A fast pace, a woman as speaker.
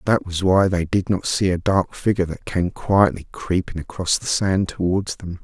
No: fast, 210 wpm; male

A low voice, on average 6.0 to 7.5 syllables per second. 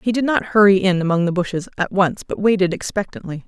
No: high, 190 Hz; 6.1 syllables/s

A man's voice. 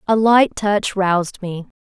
No: female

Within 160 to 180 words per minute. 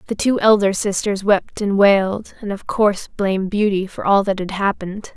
No: average, 200 wpm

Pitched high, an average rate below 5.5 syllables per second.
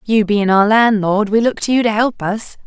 Yes: high, 215 Hz; 4.8 syllables/s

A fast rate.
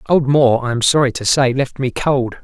Yes: fast, 245 wpm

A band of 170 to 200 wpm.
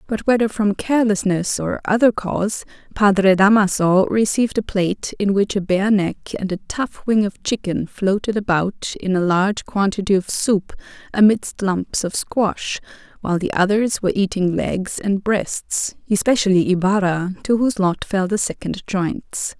No: average, 160 wpm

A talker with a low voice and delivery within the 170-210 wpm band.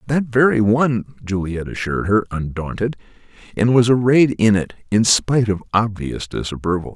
No: low, 110 Hz; average, 145 wpm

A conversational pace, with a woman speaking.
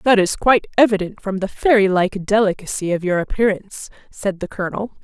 Yes: average, 180 wpm; female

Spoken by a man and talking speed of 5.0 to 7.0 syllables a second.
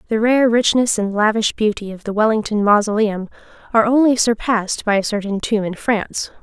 No: female; 5.6 syllables/s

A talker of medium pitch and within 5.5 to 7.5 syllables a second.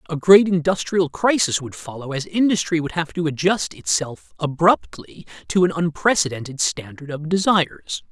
No: medium, 160 Hz; 4.9 syllables/s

